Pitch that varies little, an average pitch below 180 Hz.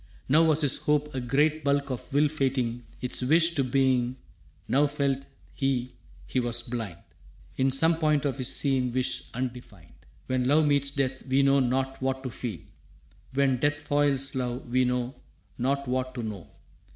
Yes: narrow, 2.1 semitones; low, 135 Hz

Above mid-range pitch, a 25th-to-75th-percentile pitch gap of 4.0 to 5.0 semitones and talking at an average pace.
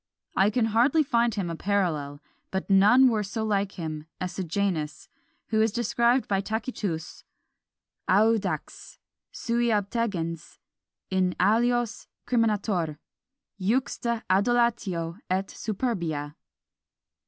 No: high, 205 Hz; average, 4.4 semitones; slow, 105 wpm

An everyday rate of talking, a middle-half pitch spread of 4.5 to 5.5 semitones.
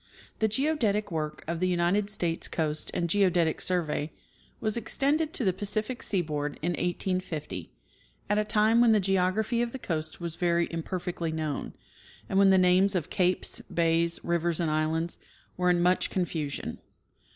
No: average, 160 wpm; average, 3.7 semitones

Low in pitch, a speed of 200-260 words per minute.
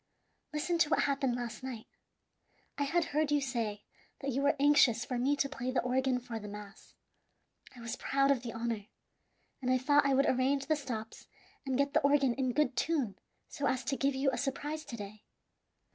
No: very high, 265 Hz; fast, 205 wpm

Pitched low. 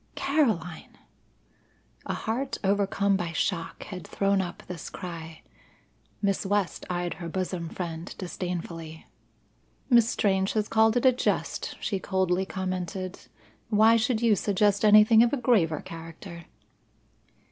No: high, 190 Hz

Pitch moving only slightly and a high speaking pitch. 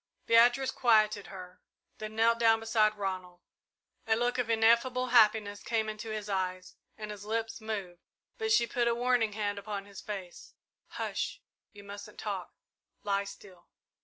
Yes: narrow, 2.3 semitones; high, 215 Hz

